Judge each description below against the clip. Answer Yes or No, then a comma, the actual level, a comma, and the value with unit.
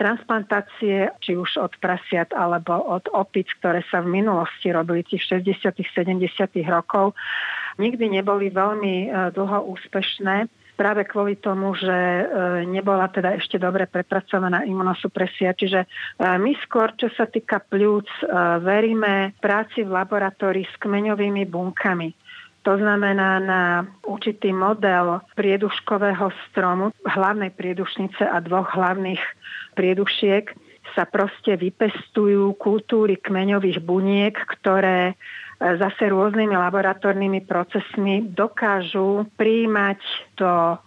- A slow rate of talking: Yes, slow, 105 wpm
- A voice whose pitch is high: Yes, high, 195 Hz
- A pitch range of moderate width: No, narrow, 1.9 semitones